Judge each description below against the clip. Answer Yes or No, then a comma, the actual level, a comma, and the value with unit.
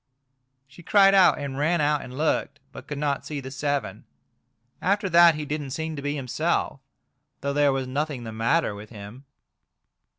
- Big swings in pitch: No, average, 3.1 semitones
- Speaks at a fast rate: No, average, 175 wpm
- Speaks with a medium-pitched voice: Yes, medium, 145 Hz